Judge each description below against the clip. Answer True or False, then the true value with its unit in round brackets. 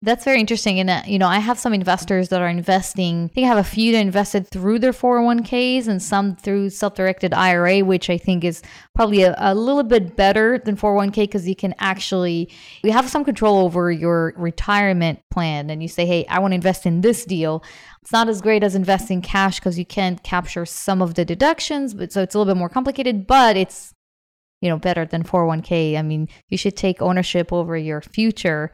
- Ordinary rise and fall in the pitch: True (3.3 semitones)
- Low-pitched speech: False (190 Hz)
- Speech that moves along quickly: True (215 wpm)